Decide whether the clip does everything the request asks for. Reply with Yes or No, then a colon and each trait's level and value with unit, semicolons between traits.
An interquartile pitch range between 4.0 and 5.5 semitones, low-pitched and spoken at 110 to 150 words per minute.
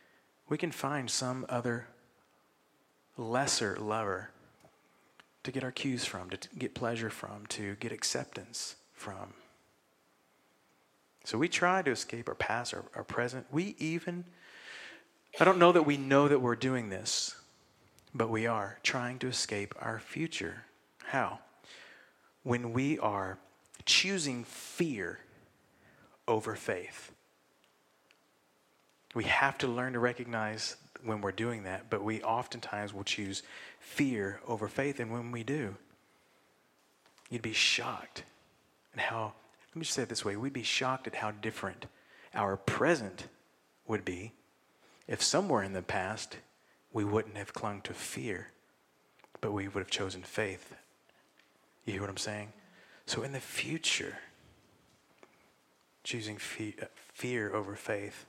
Yes: average, 4.4 semitones; low, 115 Hz; average, 140 wpm